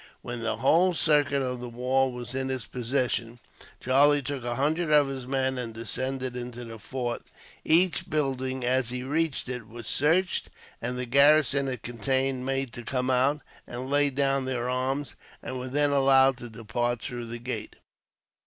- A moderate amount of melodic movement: No, narrow, 2.2 semitones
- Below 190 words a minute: Yes, average, 175 wpm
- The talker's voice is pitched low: Yes, low, 130 Hz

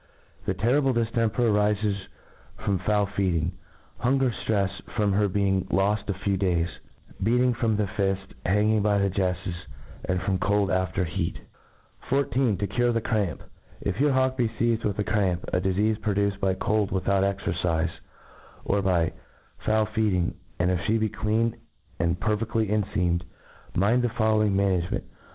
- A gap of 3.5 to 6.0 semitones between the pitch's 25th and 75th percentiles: No, narrow, 2.6 semitones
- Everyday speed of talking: Yes, average, 155 wpm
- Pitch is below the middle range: Yes, low, 100 Hz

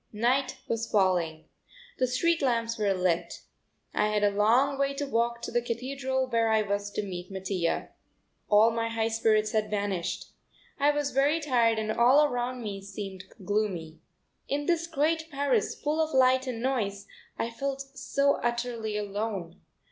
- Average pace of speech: Yes, average, 165 wpm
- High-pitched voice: Yes, high, 230 Hz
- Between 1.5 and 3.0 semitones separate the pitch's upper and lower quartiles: No, average, 4.7 semitones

